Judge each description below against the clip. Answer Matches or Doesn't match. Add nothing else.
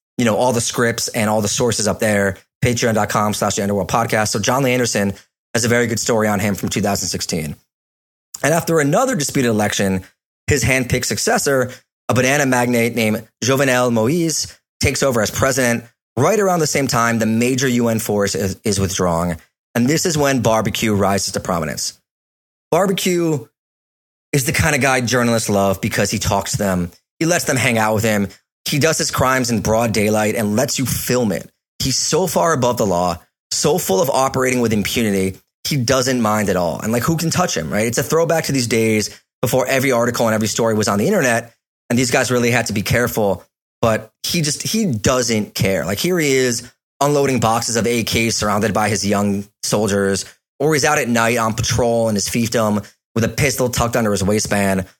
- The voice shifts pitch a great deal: Doesn't match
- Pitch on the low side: Matches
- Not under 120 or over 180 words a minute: Doesn't match